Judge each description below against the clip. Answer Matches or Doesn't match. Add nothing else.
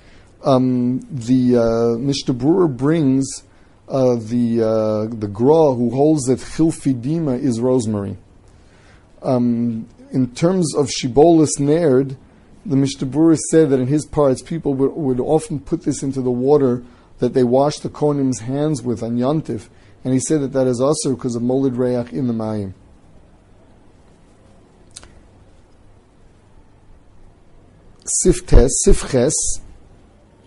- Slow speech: Matches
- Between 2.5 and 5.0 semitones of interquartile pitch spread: Doesn't match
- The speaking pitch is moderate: Doesn't match